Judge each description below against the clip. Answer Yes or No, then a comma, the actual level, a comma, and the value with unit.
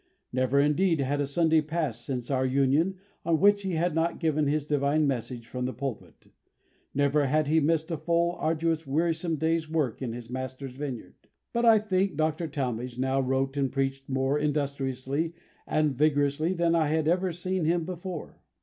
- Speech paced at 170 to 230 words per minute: Yes, average, 175 wpm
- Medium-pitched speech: Yes, medium, 150 Hz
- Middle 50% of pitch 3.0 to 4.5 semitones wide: Yes, average, 3.5 semitones